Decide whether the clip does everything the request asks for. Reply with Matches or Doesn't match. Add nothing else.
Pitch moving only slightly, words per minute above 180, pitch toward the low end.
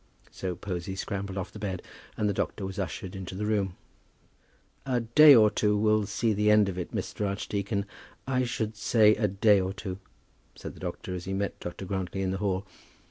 Matches